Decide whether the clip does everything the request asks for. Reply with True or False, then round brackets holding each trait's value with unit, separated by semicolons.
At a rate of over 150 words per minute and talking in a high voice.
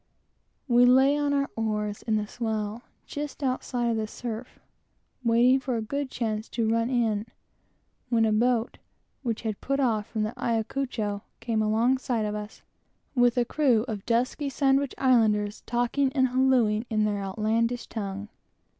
True (165 wpm; 230 Hz)